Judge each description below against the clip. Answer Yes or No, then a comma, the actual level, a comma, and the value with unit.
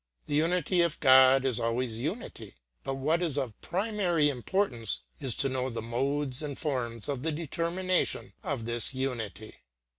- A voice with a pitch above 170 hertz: No, low, 135 Hz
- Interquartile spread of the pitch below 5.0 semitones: No, average, 5.3 semitones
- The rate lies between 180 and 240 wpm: No, average, 155 wpm